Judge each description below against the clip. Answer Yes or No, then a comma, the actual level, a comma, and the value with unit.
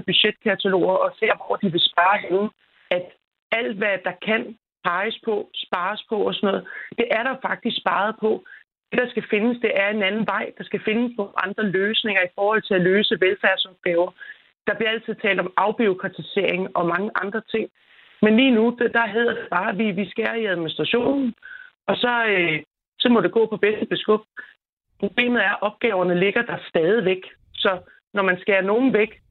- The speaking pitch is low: No, high, 210 Hz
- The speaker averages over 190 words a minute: No, average, 185 wpm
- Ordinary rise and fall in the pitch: Yes, average, 3.1 semitones